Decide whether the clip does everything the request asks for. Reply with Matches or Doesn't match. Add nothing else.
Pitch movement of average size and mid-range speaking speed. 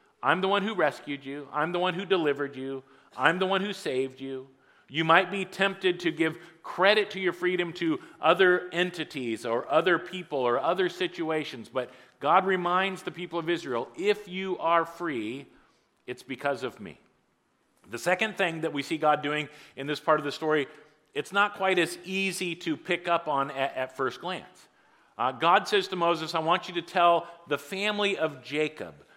Matches